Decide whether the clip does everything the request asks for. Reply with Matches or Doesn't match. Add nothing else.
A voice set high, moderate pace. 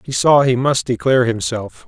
Doesn't match